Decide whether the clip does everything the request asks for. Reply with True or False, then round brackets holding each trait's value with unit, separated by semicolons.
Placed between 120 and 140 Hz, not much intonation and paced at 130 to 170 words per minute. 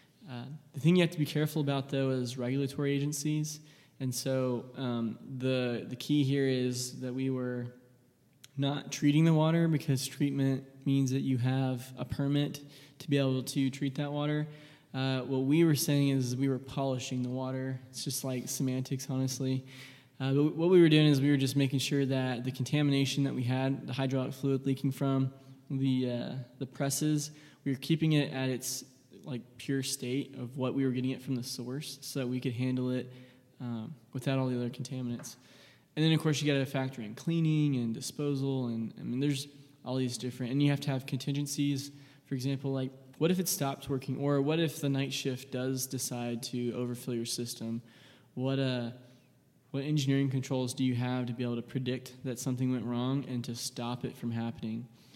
False (135 Hz; 1.8 semitones; 200 wpm)